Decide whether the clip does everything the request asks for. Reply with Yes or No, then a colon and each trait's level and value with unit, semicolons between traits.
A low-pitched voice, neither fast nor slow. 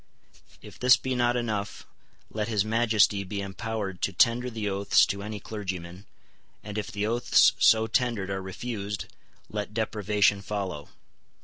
Yes: low, 105 Hz; average, 145 wpm